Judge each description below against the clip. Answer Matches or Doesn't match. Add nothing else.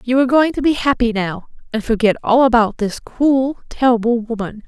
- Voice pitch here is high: Matches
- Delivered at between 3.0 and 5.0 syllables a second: Doesn't match